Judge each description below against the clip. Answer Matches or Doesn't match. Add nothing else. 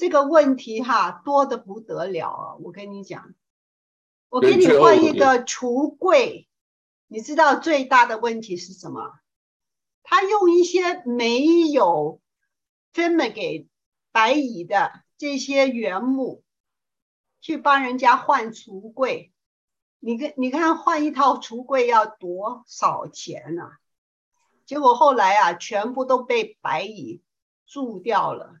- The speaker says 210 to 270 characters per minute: Doesn't match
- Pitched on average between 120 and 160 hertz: Doesn't match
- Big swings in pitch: Matches